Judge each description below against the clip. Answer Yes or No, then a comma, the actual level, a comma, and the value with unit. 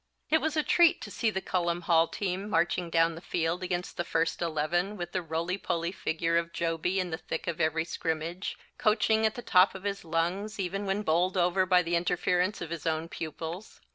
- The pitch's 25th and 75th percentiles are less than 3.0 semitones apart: Yes, narrow, 2.5 semitones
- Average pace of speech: No, fast, 210 wpm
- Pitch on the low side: No, medium, 175 Hz